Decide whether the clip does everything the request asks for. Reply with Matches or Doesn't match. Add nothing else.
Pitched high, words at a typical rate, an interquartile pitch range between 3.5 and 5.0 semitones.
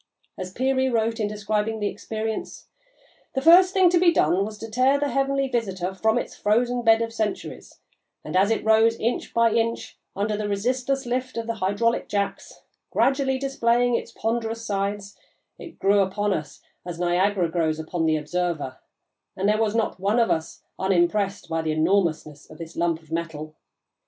Matches